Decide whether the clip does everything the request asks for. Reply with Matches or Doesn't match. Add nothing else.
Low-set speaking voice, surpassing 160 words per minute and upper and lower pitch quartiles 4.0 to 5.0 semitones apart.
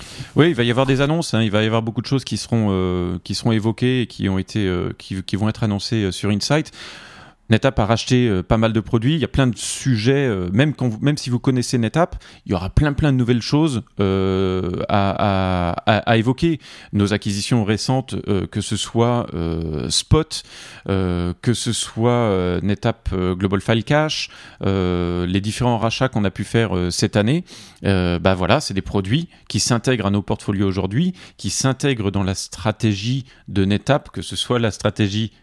Matches